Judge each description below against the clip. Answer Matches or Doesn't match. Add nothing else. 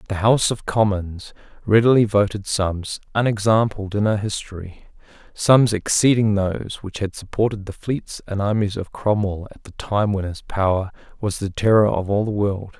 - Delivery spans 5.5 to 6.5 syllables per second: Doesn't match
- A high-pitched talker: Doesn't match